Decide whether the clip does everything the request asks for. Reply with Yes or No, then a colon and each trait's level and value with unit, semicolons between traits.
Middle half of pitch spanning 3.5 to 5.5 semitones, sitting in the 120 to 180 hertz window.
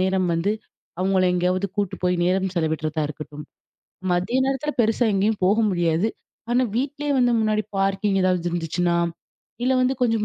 No: average, 4.0 semitones; high, 190 Hz